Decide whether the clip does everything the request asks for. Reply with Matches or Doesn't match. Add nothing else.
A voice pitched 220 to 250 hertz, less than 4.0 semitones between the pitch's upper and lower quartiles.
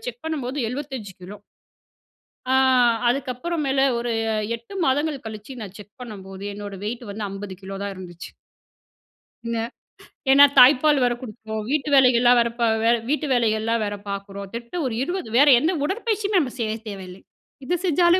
Doesn't match